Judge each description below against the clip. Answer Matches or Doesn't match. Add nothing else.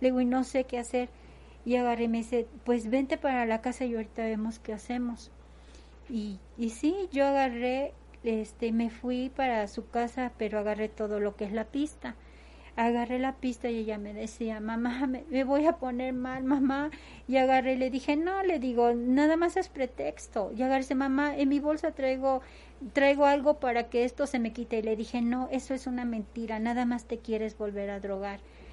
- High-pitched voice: Matches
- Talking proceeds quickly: Matches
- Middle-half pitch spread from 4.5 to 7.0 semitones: Doesn't match